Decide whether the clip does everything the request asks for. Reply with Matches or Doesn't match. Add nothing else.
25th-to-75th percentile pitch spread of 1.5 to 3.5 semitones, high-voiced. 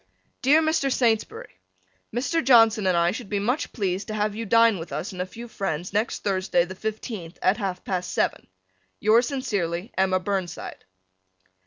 Doesn't match